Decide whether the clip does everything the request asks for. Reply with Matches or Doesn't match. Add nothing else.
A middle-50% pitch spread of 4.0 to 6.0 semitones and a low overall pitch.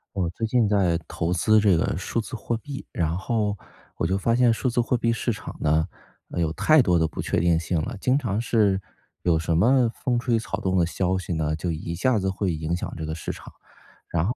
Matches